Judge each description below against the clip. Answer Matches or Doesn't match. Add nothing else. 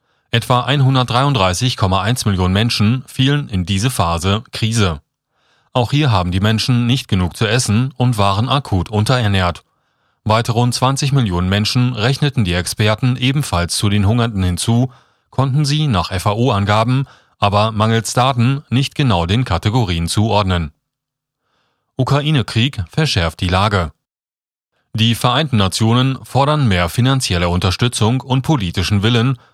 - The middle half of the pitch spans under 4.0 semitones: Doesn't match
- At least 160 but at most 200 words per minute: Doesn't match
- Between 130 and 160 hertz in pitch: Doesn't match